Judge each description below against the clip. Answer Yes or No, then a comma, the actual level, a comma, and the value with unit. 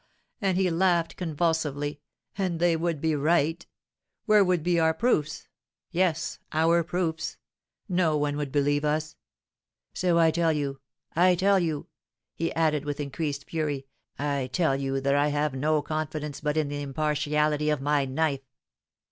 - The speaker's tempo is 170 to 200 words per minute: No, average, 155 wpm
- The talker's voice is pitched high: No, medium, 155 Hz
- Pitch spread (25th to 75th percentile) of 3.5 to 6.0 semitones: No, narrow, 2.6 semitones